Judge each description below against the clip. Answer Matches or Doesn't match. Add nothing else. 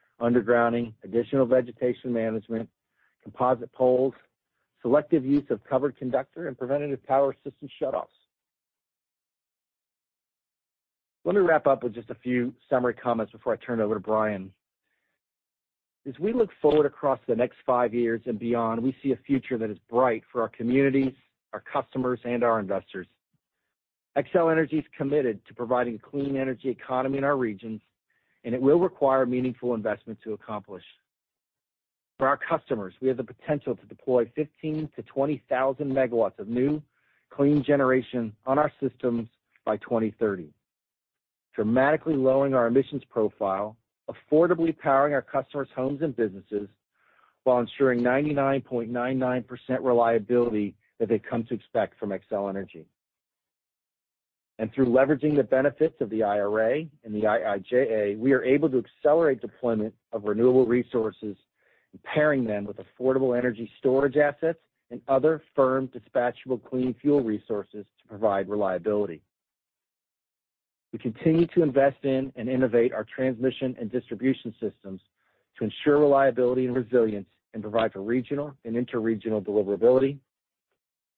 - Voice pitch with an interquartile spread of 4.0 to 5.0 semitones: Doesn't match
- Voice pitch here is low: Matches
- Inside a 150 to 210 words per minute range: Doesn't match